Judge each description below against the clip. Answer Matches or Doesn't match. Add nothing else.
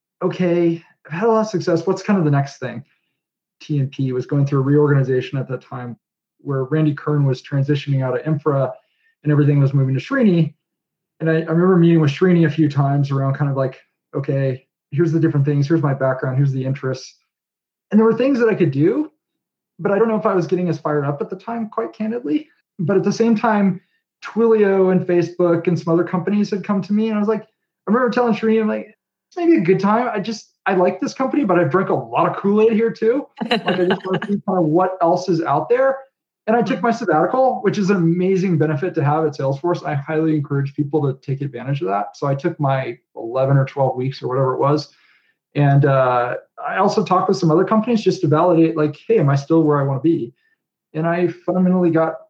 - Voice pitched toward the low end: Doesn't match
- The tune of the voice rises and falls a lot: Matches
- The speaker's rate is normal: Doesn't match